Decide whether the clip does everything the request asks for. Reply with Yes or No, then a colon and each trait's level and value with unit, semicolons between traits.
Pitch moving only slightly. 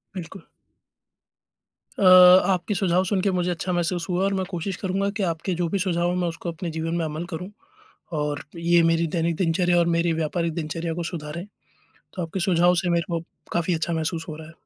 Yes: narrow, 1.7 semitones